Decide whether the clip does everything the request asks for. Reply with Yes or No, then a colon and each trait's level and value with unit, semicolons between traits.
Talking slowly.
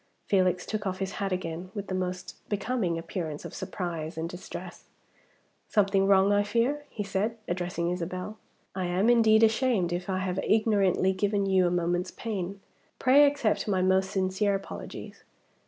No: average, 160 wpm